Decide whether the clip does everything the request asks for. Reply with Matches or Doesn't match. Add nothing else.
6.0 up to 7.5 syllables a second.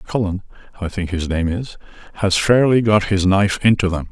Doesn't match